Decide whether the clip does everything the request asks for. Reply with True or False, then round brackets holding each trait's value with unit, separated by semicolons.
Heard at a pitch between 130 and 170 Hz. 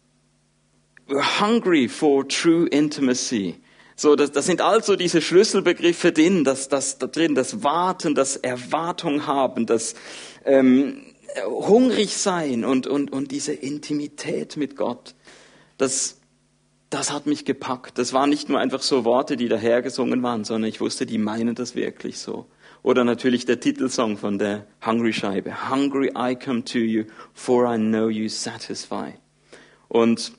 True (135 Hz)